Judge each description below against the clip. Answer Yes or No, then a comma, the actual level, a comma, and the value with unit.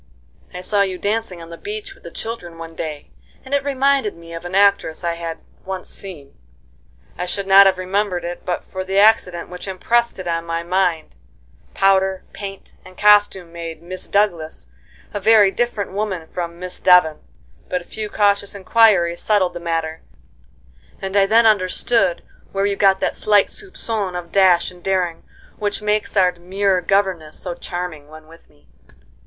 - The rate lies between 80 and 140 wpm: No, average, 175 wpm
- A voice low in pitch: No, medium, 185 Hz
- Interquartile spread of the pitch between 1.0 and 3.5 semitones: Yes, average, 3.0 semitones